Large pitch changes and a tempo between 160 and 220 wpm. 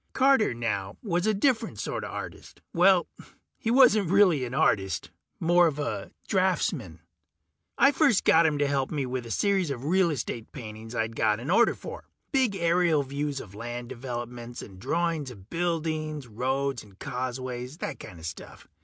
Yes: wide, 6.8 semitones; average, 170 wpm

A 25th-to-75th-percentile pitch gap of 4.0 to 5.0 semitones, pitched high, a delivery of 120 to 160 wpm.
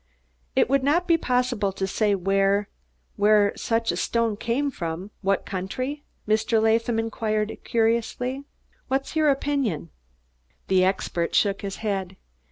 Yes: average, 4.3 semitones; high, 220 Hz; slow, 135 wpm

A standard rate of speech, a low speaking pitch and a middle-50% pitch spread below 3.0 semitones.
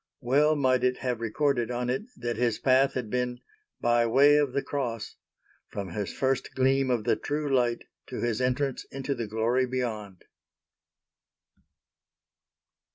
Yes: average, 150 wpm; low, 125 Hz; narrow, 2.4 semitones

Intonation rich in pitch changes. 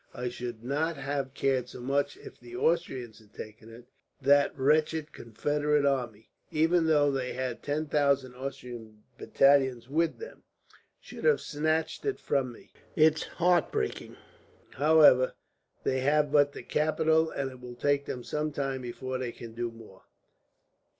No: average, 3.5 semitones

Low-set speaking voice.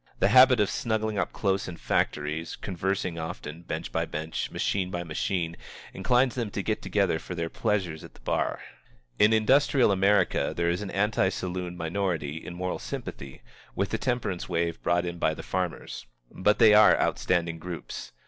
Yes: very low, 90 Hz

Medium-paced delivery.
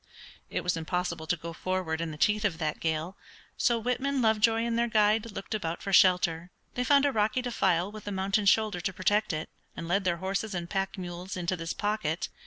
No: fast, 210 wpm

